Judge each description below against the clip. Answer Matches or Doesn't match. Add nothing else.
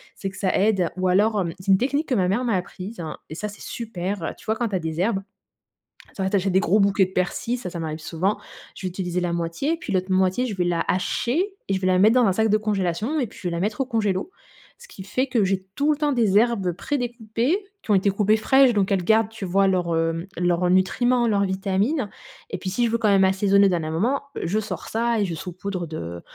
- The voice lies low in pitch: Doesn't match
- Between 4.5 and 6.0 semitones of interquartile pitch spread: Doesn't match